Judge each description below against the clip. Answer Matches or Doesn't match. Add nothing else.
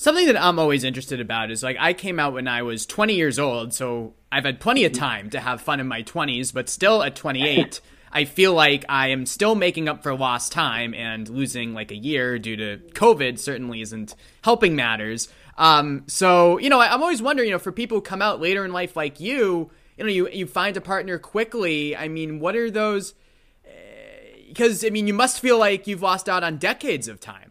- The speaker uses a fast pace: Matches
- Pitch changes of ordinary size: Doesn't match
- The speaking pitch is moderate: Matches